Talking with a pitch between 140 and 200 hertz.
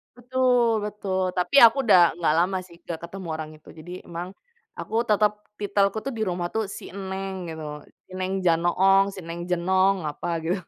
Yes: high, 190 Hz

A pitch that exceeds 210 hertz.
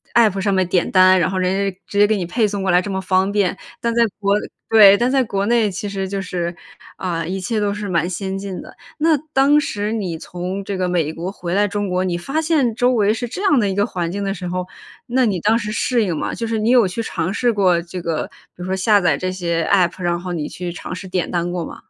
No: high, 195 Hz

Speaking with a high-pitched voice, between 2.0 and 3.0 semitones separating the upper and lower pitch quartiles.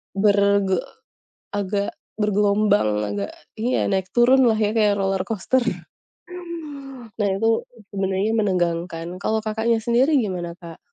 Yes: high, 205 Hz; average, 2.7 semitones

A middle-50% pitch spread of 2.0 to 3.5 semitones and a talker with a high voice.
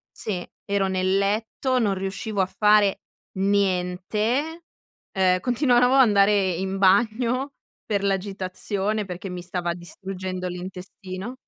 Yes: average, 2.7 semitones; high, 195 Hz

